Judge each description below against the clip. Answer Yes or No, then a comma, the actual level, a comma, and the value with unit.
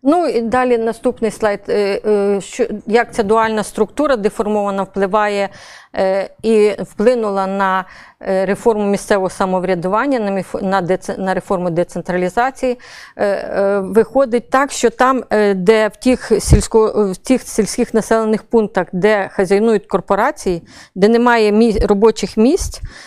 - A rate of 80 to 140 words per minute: Yes, slow, 110 wpm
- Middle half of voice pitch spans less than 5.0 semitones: Yes, average, 2.9 semitones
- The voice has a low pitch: No, high, 210 Hz